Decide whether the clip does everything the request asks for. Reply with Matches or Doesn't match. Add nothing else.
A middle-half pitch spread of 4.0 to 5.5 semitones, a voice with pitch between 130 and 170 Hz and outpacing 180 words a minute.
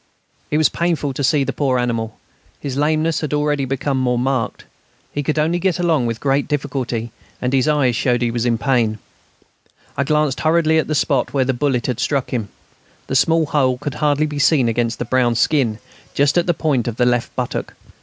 Doesn't match